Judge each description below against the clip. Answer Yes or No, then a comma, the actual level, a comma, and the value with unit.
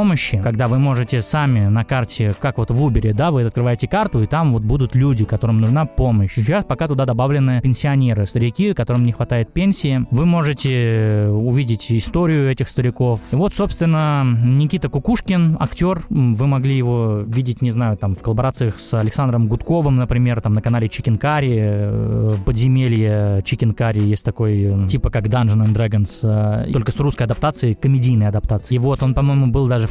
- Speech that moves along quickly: Yes, fast, 170 wpm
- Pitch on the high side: No, low, 125 Hz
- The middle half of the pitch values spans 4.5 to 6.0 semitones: No, average, 3.5 semitones